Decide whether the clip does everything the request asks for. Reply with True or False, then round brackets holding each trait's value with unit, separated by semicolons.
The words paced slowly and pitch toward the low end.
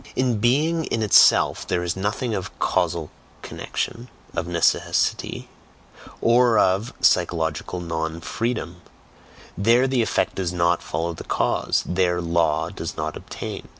True (130 wpm; 90 Hz)